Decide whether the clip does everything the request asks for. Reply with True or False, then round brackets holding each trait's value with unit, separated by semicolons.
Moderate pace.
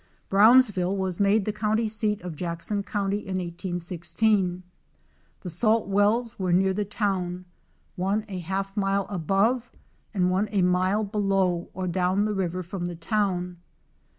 True (150 wpm)